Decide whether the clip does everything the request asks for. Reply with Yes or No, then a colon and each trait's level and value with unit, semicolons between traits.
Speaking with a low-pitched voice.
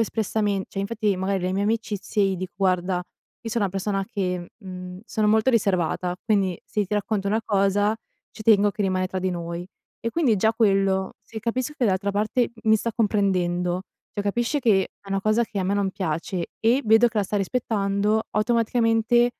No: high, 200 Hz